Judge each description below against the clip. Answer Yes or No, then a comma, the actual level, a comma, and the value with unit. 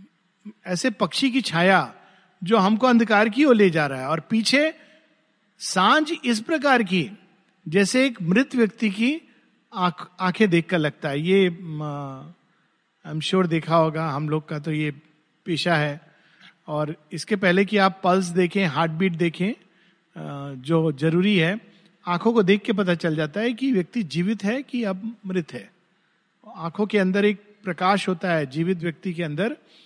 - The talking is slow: No, average, 155 wpm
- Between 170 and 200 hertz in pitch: Yes, medium, 185 Hz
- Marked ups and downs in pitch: No, average, 4.2 semitones